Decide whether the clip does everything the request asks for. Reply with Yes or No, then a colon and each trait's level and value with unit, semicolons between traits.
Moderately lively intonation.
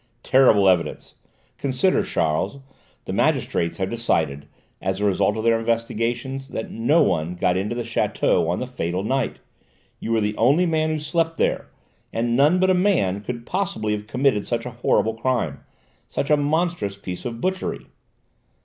No: wide, 5.8 semitones